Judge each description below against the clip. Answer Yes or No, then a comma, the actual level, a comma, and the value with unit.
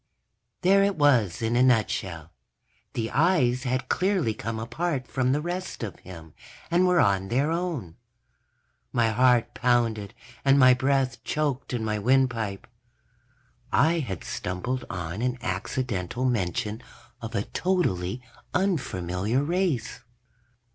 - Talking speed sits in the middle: No, slow, 130 wpm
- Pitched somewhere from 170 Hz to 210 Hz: No, low, 125 Hz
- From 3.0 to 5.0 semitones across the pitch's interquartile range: No, wide, 5.6 semitones